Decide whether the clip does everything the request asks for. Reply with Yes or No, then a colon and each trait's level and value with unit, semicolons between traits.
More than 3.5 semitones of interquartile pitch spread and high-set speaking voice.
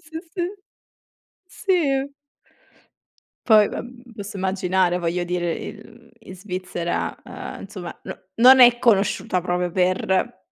Yes: average, 5.2 semitones; high, 200 Hz